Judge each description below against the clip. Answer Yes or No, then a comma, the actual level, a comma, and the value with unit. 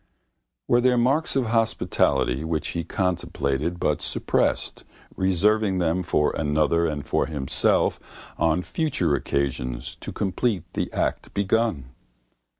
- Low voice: Yes, very low, 85 Hz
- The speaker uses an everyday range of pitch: No, wide, 6.5 semitones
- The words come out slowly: Yes, slow, 120 wpm